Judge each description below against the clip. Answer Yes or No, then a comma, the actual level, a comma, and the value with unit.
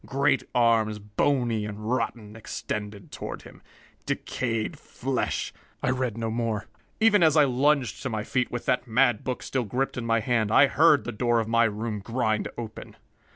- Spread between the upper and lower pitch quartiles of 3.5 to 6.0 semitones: No, average, 2.9 semitones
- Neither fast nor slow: Yes, average, 180 wpm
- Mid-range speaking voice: No, low, 115 Hz